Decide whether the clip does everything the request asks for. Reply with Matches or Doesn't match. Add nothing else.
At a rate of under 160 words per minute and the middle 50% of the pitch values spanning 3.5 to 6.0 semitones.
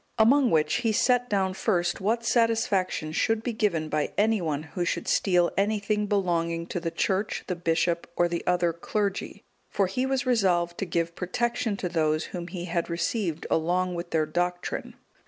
Doesn't match